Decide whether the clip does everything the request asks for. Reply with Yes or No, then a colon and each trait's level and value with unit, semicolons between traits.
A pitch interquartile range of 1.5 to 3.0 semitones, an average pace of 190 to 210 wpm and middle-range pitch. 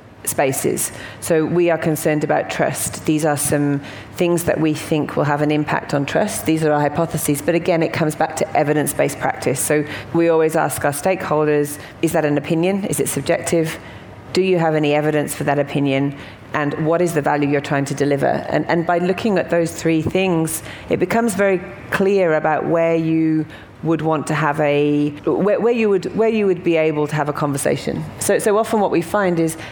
Yes: average, 2.7 semitones; fast, 205 wpm; medium, 155 Hz